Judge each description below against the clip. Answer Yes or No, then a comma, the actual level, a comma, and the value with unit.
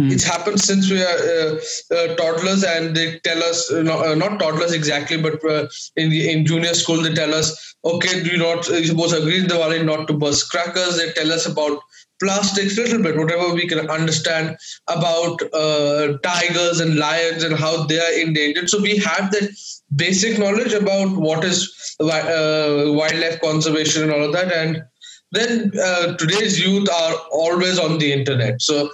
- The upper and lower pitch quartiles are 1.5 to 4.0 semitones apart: Yes, average, 2.8 semitones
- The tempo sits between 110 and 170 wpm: No, average, 185 wpm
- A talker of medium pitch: Yes, medium, 165 Hz